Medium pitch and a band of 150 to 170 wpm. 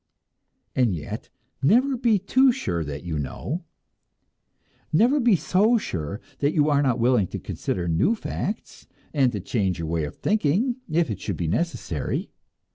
Yes: medium, 145 Hz; average, 160 wpm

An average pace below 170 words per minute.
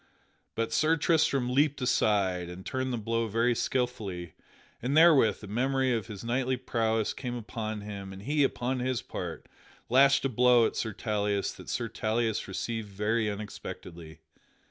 Yes: average, 160 wpm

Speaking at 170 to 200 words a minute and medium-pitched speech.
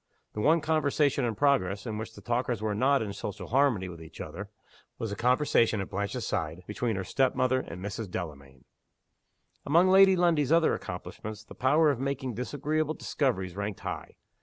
No: average, 180 wpm; low, 120 Hz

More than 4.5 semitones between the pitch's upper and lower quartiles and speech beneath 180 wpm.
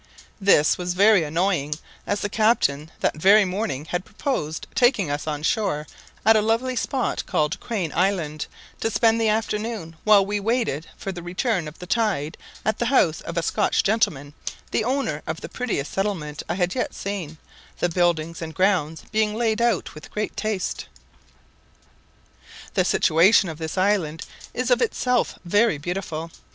Yes: wide, 5.4 semitones; average, 165 wpm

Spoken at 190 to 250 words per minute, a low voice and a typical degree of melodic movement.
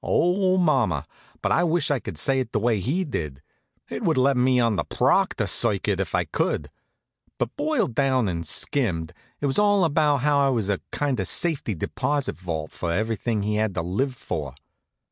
No: average, 195 wpm; low, 125 Hz; wide, 6.7 semitones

